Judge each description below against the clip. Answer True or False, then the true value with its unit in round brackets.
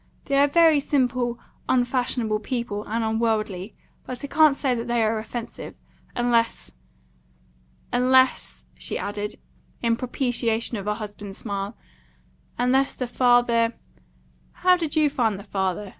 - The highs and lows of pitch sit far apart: False (3.1 semitones)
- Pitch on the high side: True (235 Hz)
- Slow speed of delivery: True (130 wpm)